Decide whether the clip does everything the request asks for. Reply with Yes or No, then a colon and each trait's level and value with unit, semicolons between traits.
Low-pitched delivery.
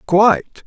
No: medium, 180 Hz